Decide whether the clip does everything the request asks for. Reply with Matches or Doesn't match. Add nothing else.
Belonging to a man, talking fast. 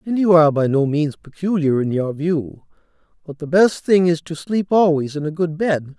Matches